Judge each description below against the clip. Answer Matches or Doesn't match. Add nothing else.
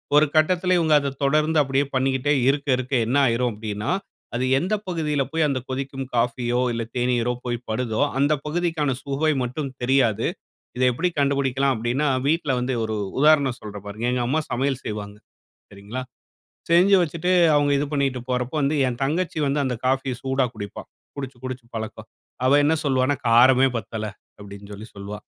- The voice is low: Matches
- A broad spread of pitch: Doesn't match